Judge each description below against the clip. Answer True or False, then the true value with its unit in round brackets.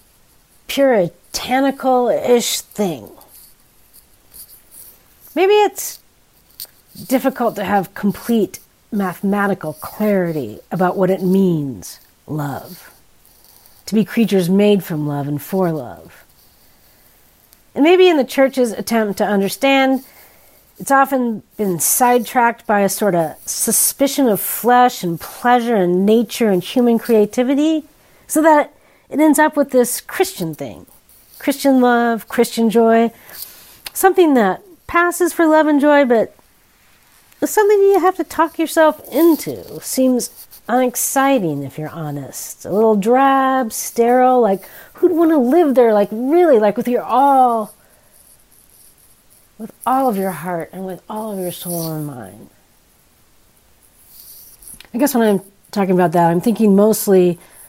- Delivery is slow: True (130 wpm)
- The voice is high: True (230 Hz)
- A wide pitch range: True (6.1 semitones)